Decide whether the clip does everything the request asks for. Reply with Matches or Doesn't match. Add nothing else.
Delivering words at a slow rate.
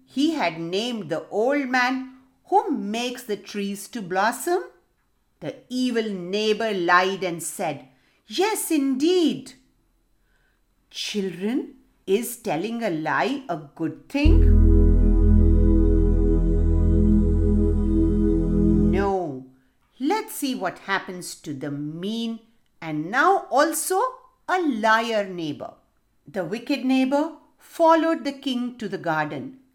Matches